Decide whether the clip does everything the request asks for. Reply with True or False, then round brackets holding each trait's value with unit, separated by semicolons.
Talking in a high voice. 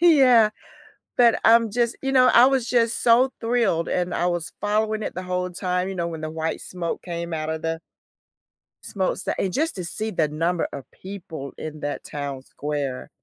False (180 Hz)